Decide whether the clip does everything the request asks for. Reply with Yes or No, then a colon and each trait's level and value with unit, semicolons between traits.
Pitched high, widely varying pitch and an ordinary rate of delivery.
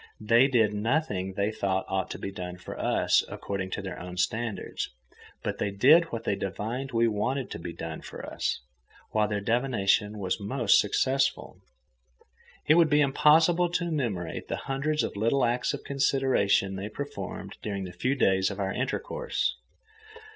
No: low, 110 Hz; wide, 5.7 semitones; average, 165 wpm